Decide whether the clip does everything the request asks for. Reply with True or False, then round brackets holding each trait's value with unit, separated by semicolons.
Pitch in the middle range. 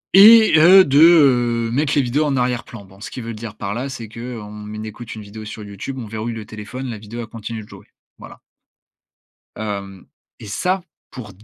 False (115 Hz)